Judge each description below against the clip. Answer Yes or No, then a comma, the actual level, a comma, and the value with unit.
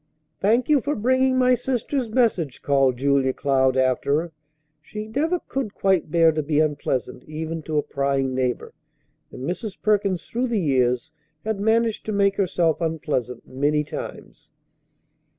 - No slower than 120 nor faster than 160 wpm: Yes, average, 150 wpm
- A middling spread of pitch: No, wide, 7.8 semitones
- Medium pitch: Yes, medium, 165 Hz